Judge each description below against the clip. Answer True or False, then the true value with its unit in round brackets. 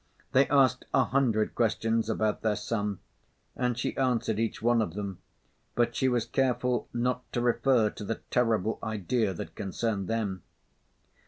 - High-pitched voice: False (115 Hz)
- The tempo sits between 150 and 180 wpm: True (155 wpm)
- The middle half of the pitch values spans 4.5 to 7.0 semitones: False (2.5 semitones)